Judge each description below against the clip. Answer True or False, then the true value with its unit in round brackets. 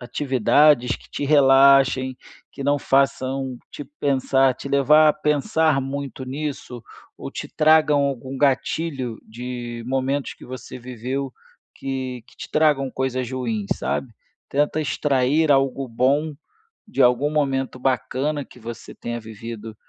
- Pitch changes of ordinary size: False (2.2 semitones)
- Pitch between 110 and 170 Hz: True (135 Hz)